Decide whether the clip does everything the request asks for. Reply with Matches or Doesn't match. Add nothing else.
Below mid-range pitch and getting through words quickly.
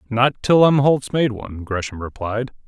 Doesn't match